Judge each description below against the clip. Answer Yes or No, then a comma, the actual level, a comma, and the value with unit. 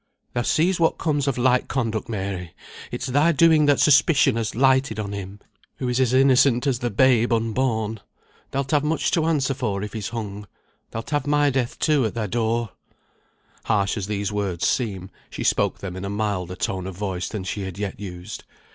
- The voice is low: Yes, low, 115 Hz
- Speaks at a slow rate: No, average, 195 wpm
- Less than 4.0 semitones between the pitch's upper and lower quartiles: No, average, 4.9 semitones